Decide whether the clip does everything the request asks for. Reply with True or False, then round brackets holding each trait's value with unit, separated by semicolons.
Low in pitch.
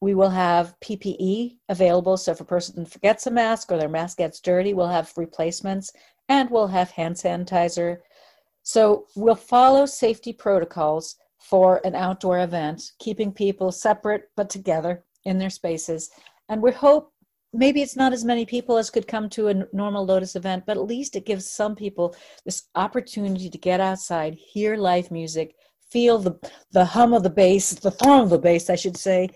False (195 Hz)